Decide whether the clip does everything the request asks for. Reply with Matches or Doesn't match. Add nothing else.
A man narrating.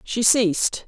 Doesn't match